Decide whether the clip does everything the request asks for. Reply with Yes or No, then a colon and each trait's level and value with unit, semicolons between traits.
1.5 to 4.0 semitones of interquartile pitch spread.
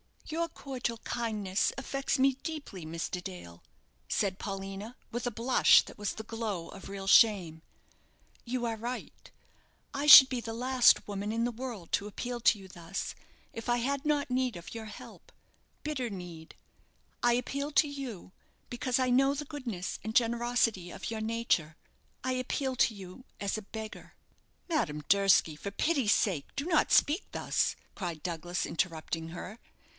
No: average, 5.0 semitones